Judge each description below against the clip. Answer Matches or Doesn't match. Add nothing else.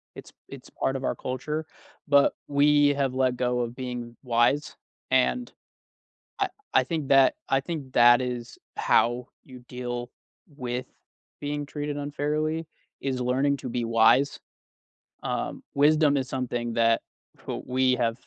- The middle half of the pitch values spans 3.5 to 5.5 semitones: Doesn't match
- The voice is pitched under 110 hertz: Doesn't match